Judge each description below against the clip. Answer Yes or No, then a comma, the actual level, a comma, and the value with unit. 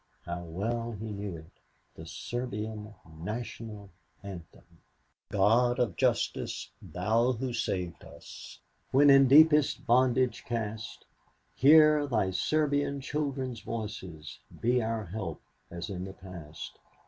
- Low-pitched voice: Yes, low, 110 Hz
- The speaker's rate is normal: No, slow, 115 wpm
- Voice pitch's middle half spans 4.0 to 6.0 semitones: Yes, average, 5.0 semitones